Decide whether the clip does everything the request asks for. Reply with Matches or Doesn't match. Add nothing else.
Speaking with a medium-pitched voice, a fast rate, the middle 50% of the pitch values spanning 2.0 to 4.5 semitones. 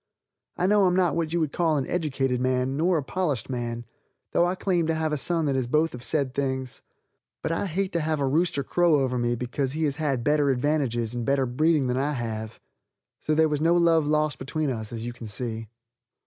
Matches